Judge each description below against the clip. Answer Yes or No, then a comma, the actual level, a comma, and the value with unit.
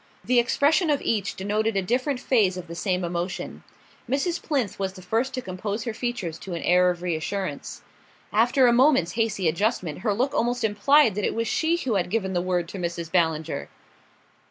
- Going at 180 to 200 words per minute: Yes, average, 195 wpm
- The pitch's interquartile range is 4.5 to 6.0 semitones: Yes, average, 5.2 semitones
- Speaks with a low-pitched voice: No, high, 205 Hz